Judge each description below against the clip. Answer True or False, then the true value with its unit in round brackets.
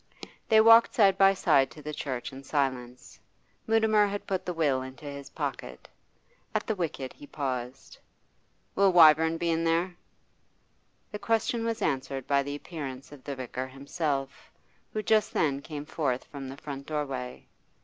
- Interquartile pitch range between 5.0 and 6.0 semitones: True (5.3 semitones)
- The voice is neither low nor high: True (145 Hz)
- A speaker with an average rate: True (160 wpm)